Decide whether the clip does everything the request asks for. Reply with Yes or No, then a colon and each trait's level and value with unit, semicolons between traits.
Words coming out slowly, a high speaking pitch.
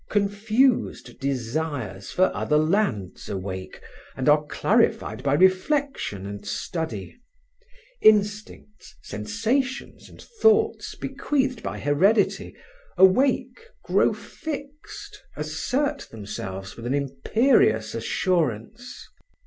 No: slow, 90 wpm; medium, 160 Hz